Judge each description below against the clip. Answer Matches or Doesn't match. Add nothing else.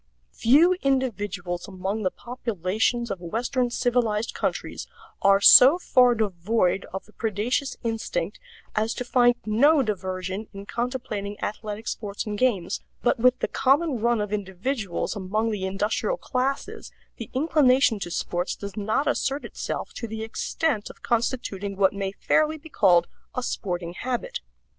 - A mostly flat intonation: Doesn't match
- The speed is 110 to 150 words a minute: Matches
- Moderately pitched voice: Doesn't match